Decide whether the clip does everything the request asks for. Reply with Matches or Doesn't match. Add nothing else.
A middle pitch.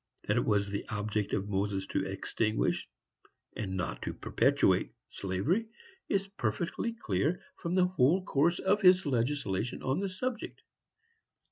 Doesn't match